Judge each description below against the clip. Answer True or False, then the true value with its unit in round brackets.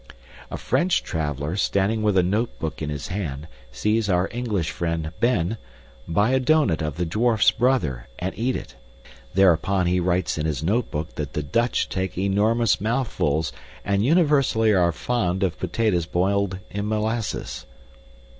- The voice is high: False (95 Hz)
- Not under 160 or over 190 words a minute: False (150 wpm)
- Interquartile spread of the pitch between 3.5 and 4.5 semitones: False (5.4 semitones)